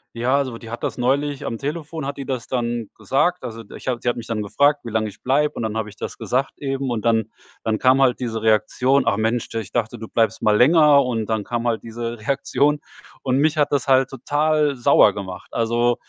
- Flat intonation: No, average, 3.6 semitones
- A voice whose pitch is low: Yes, low, 120 Hz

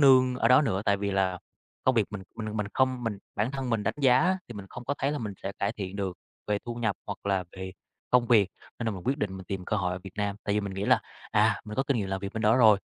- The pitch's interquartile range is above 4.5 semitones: No, average, 4.0 semitones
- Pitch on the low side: Yes, low, 105 Hz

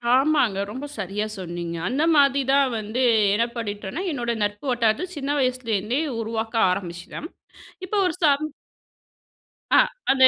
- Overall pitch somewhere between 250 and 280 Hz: No, high, 235 Hz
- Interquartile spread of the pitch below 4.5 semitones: No, average, 5.2 semitones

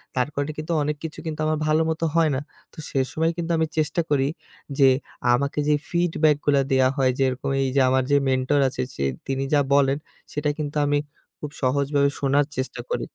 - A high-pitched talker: No, medium, 145 Hz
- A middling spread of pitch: No, narrow, 2.3 semitones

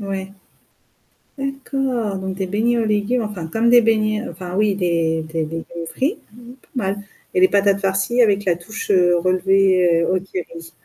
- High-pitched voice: Yes, high, 195 Hz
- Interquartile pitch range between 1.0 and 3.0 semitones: No, average, 3.4 semitones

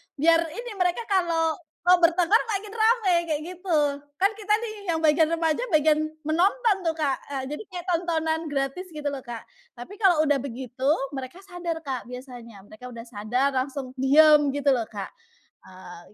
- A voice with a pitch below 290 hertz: No, very high, 310 Hz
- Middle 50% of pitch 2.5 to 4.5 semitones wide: No, average, 5.1 semitones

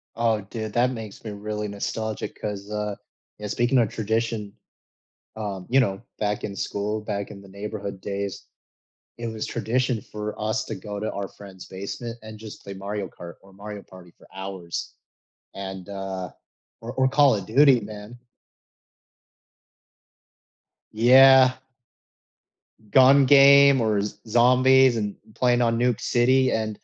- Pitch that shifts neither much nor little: Yes, average, 3.1 semitones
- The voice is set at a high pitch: No, low, 110 Hz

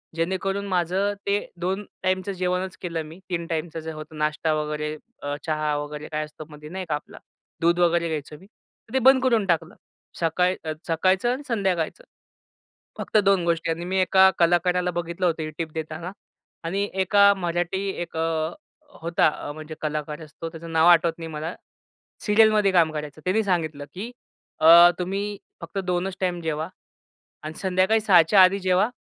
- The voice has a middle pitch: Yes, medium, 175 Hz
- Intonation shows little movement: No, average, 3.1 semitones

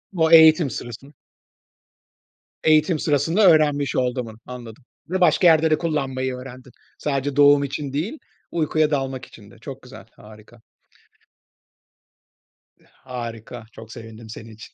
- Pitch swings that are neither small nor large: Yes, average, 4.3 semitones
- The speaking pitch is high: No, low, 135 Hz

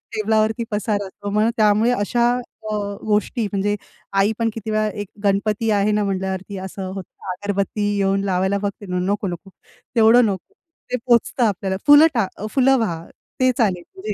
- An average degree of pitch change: No, narrow, 2.2 semitones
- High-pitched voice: Yes, high, 205 Hz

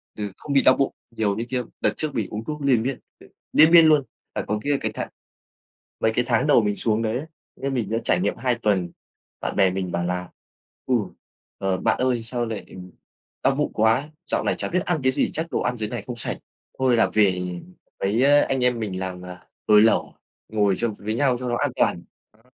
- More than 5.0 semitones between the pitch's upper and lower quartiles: No, average, 4.4 semitones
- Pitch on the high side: No, low, 115 Hz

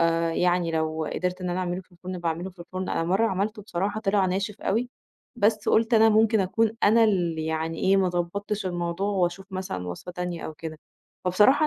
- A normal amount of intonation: Yes, average, 3.1 semitones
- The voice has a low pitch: No, medium, 185 Hz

